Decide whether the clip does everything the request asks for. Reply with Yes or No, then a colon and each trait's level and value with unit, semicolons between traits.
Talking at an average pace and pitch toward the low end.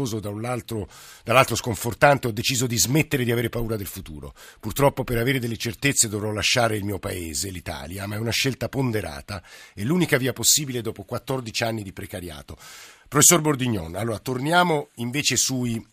Yes: average, 160 wpm; low, 115 Hz